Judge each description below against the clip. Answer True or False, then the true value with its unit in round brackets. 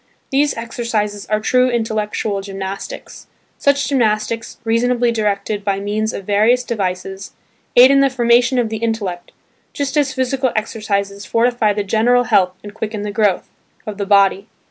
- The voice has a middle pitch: False (220 Hz)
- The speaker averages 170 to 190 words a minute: False (150 wpm)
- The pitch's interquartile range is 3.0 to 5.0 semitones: True (3.3 semitones)